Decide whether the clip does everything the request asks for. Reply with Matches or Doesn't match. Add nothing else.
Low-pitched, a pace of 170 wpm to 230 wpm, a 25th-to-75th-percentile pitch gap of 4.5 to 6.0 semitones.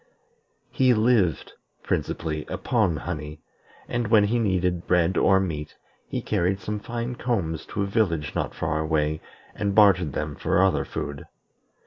Doesn't match